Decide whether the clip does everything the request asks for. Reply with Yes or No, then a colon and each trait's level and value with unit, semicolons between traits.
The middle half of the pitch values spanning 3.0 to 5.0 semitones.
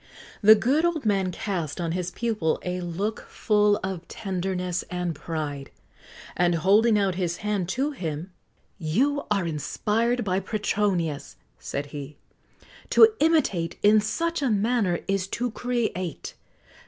Yes: average, 4.4 semitones